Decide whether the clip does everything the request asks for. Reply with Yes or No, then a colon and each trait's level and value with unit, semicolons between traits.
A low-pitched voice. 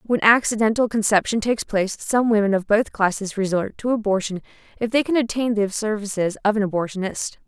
No: high, 210 Hz